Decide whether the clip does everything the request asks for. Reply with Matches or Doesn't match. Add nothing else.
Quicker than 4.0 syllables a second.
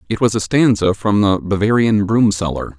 Matches